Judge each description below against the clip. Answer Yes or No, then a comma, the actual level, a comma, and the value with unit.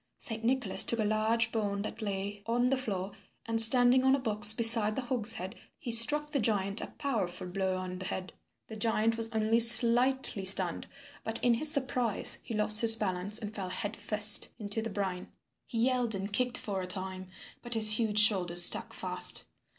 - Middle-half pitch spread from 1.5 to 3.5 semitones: Yes, average, 2.9 semitones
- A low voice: No, high, 220 Hz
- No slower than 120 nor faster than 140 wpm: No, average, 190 wpm